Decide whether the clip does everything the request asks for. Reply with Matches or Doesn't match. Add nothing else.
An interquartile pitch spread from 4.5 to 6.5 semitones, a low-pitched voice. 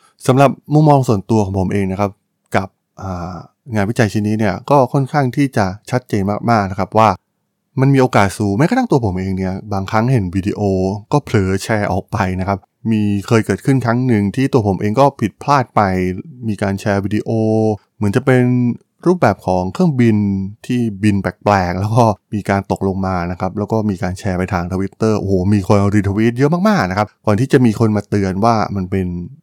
Doesn't match